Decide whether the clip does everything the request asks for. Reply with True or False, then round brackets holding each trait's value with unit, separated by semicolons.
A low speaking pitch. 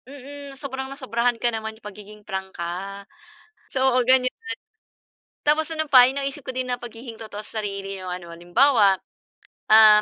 False (230 Hz)